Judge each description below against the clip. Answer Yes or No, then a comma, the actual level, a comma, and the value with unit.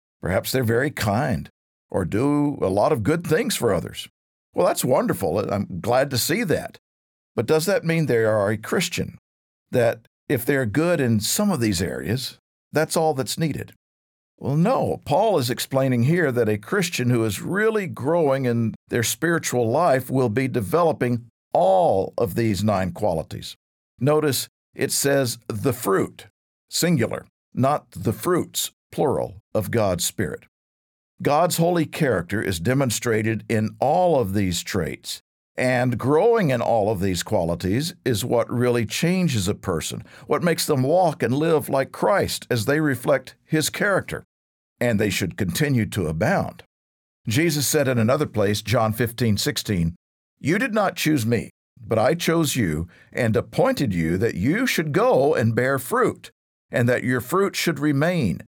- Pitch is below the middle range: Yes, low, 125 Hz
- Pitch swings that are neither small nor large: No, wide, 6.3 semitones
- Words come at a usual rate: Yes, average, 160 wpm